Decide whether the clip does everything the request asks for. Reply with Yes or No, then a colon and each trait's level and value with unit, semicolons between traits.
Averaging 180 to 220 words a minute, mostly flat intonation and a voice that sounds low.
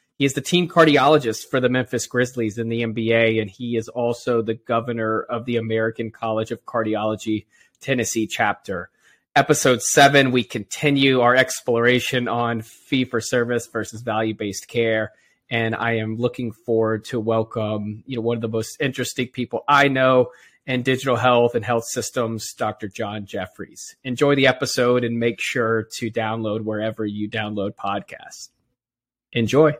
No: average, 160 wpm; narrow, 2.1 semitones; low, 120 Hz